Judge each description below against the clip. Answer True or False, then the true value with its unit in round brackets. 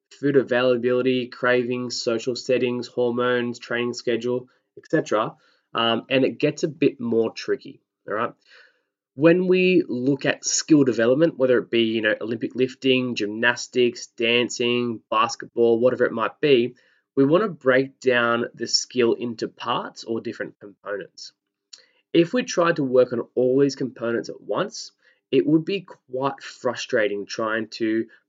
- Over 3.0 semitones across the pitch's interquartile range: False (2.6 semitones)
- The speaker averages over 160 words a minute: False (145 wpm)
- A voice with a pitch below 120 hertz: False (125 Hz)